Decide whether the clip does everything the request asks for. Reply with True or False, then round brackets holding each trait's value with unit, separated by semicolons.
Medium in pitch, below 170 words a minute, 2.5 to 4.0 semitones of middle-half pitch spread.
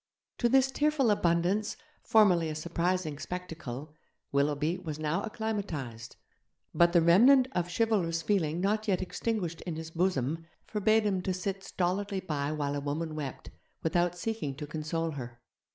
False (170 Hz; 150 wpm; 4.7 semitones)